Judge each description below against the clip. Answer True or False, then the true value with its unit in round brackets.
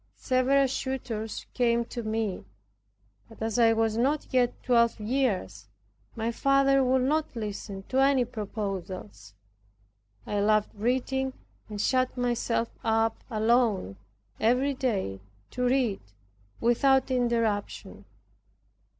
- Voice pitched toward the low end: False (235 Hz)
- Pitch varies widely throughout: False (3.3 semitones)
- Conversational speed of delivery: False (110 wpm)